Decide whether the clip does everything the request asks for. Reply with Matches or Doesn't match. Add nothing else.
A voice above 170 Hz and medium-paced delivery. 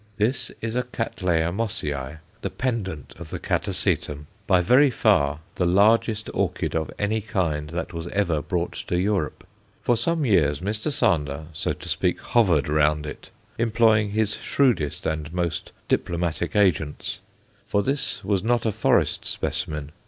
Doesn't match